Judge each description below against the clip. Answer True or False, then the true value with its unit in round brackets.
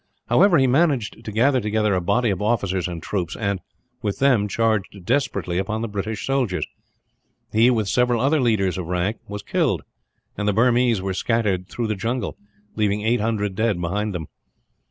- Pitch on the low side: True (105 Hz)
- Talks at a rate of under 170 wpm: False (175 wpm)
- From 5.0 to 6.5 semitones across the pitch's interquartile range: False (3.5 semitones)